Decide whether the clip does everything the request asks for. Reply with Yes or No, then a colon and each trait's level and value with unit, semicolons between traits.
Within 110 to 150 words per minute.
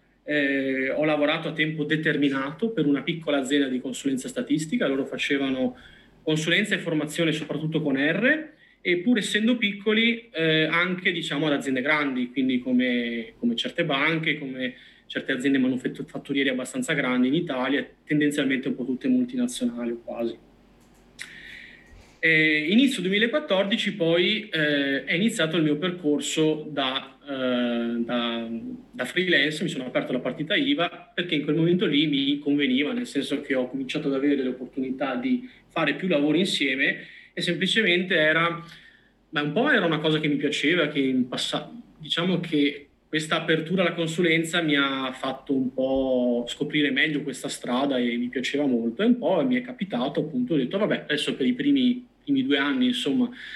No: average, 160 wpm